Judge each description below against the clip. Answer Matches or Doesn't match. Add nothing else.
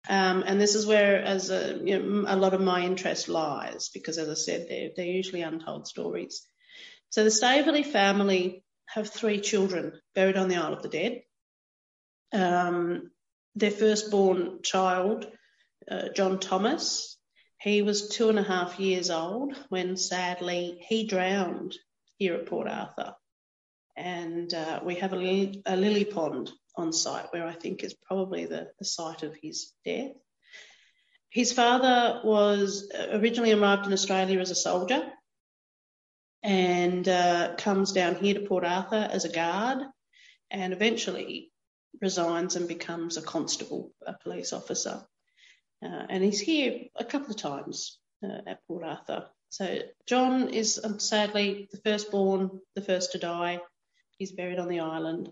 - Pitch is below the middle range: Doesn't match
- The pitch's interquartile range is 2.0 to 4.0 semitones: Matches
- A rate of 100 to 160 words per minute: Matches